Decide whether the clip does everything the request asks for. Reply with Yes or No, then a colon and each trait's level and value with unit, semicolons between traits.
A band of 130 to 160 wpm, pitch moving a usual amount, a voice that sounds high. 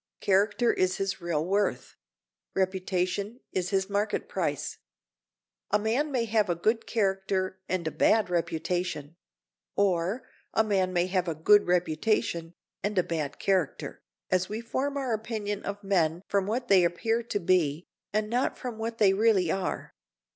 Yes: average, 155 wpm; average, 3.4 semitones; high, 195 Hz